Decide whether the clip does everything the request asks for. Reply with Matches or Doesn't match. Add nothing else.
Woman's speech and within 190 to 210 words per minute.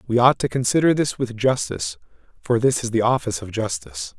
Doesn't match